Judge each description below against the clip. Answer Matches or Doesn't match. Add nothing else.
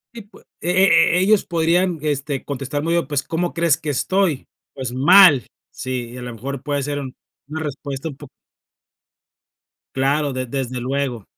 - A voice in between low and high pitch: Matches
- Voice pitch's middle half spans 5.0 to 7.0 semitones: Doesn't match